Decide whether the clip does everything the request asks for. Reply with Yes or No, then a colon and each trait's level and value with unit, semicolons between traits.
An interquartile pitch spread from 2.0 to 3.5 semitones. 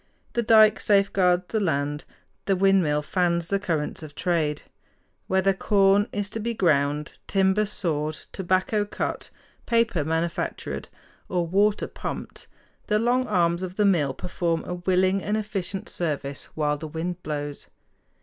No: average, 4.1 semitones